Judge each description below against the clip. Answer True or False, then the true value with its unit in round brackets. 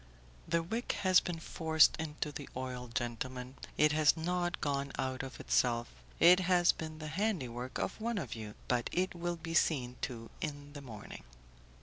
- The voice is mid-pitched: True (150 Hz)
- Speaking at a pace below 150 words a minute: False (175 wpm)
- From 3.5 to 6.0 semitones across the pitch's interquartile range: True (5.2 semitones)